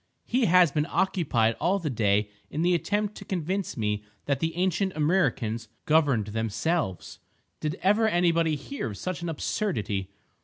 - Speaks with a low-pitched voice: No, medium, 160 Hz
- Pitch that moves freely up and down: Yes, wide, 8.3 semitones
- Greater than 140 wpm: Yes, average, 150 wpm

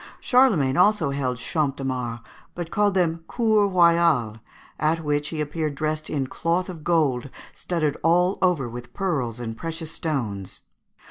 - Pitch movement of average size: Yes, average, 4.5 semitones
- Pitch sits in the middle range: Yes, medium, 155 Hz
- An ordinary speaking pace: Yes, average, 150 wpm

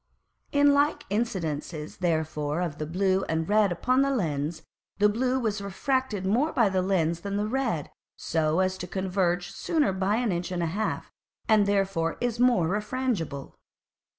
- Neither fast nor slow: Yes, average, 165 wpm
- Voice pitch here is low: No, high, 190 Hz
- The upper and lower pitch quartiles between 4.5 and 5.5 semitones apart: Yes, average, 5.1 semitones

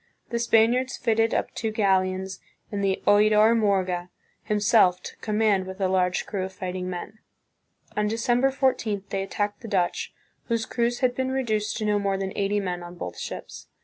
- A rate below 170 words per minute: No, average, 180 wpm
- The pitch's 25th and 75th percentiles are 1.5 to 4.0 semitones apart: Yes, average, 3.0 semitones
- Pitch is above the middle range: Yes, high, 205 Hz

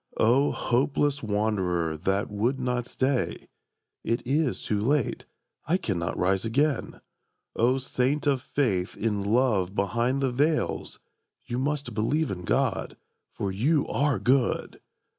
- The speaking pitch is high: No, low, 120 Hz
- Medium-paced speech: No, slow, 130 wpm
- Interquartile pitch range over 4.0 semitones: Yes, average, 5.2 semitones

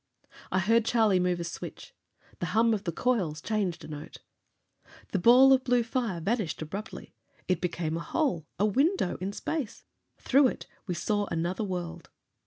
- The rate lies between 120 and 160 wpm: No, average, 170 wpm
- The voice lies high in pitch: Yes, high, 200 Hz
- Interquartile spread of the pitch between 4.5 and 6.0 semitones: Yes, average, 5.2 semitones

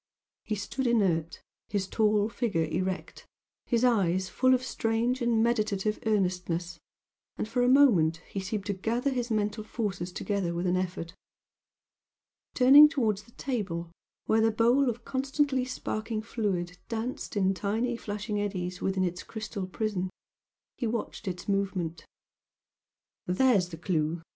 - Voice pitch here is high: Yes, high, 210 Hz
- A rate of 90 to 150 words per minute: Yes, average, 140 wpm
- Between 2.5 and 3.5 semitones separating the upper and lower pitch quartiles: No, average, 4.3 semitones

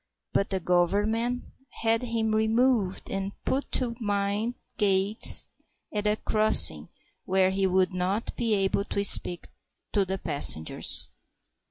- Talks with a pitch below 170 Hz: No, high, 205 Hz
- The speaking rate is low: Yes, slow, 130 wpm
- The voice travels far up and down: No, average, 2.7 semitones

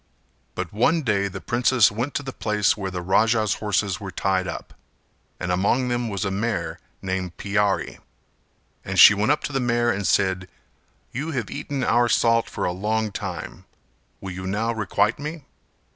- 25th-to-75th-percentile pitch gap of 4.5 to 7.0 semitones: No, average, 3.8 semitones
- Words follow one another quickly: No, average, 175 wpm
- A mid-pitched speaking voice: No, low, 105 Hz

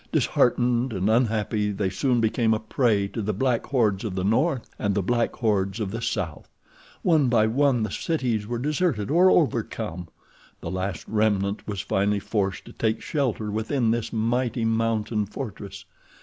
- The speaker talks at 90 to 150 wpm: No, average, 165 wpm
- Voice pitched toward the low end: Yes, low, 110 Hz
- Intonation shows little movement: No, average, 3.1 semitones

